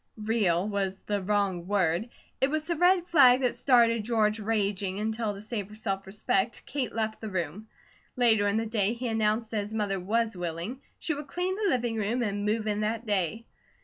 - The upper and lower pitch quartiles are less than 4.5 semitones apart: Yes, average, 2.8 semitones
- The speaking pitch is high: Yes, high, 215 Hz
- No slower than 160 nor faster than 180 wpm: No, average, 200 wpm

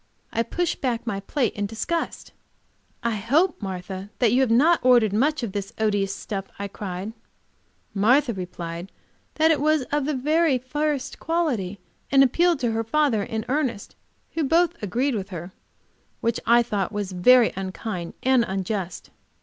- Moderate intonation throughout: No, wide, 6.1 semitones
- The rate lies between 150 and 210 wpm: Yes, average, 160 wpm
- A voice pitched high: Yes, high, 230 Hz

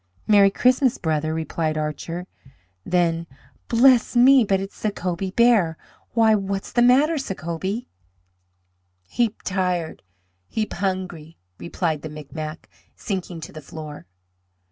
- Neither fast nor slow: No, slow, 115 wpm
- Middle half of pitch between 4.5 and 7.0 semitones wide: Yes, wide, 5.4 semitones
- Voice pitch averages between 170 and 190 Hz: Yes, medium, 185 Hz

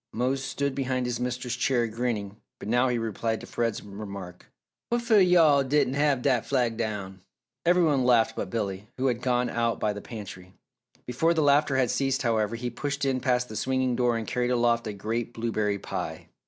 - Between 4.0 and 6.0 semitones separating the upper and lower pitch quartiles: No, average, 3.2 semitones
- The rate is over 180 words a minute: Yes, average, 195 wpm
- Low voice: Yes, low, 120 Hz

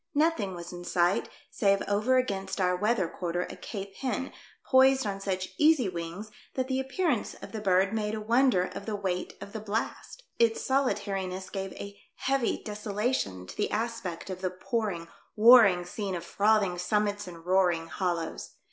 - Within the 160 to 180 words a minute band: Yes, average, 175 wpm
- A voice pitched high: Yes, high, 200 Hz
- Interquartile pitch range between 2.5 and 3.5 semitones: No, average, 3.9 semitones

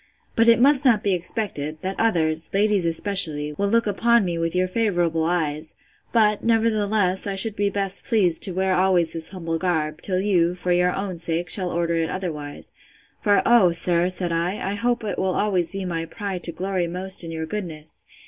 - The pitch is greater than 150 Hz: Yes, medium, 185 Hz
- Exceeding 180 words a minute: Yes, average, 195 wpm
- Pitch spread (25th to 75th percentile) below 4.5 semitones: Yes, average, 3.5 semitones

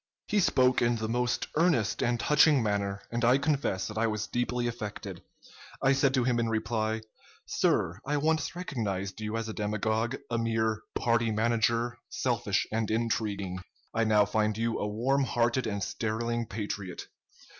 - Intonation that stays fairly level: Yes, narrow, 2.2 semitones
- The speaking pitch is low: Yes, low, 115 Hz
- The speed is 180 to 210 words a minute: No, average, 165 wpm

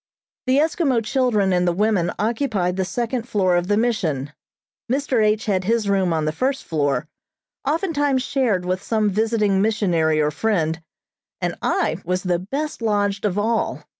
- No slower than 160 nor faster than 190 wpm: Yes, average, 165 wpm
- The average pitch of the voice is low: No, high, 210 Hz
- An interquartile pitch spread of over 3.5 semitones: Yes, average, 4.8 semitones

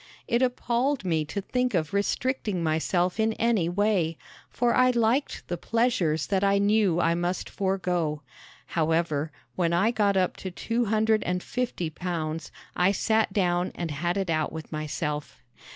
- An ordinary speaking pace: Yes, average, 160 wpm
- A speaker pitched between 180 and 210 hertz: Yes, medium, 185 Hz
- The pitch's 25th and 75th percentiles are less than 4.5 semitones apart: No, average, 4.9 semitones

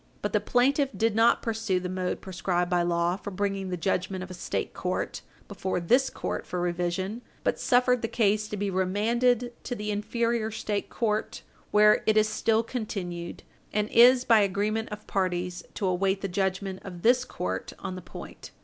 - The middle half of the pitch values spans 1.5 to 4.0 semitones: Yes, average, 3.6 semitones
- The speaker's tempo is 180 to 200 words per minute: Yes, average, 185 wpm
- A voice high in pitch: Yes, high, 205 Hz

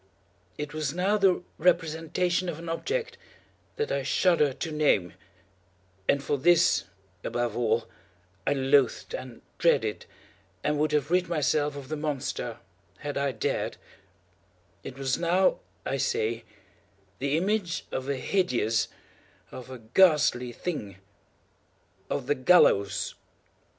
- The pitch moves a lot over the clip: Yes, wide, 5.8 semitones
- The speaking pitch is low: No, medium, 145 Hz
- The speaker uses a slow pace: Yes, slow, 115 wpm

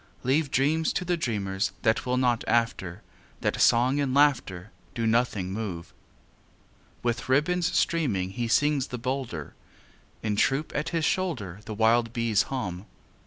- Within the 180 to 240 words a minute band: No, average, 145 wpm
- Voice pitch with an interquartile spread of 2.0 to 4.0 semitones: No, average, 5.1 semitones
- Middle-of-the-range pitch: No, low, 120 Hz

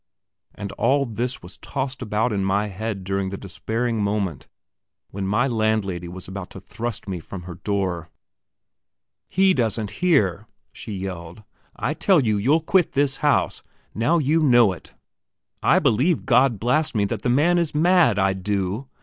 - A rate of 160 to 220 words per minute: Yes, average, 165 wpm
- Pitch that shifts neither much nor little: No, wide, 5.7 semitones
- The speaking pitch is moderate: No, low, 110 Hz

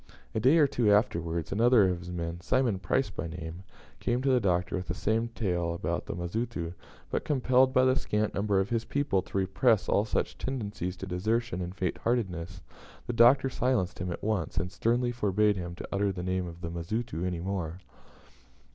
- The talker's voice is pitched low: Yes, low, 100 Hz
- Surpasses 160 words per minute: Yes, average, 200 wpm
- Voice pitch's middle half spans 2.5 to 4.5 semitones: No, average, 5.0 semitones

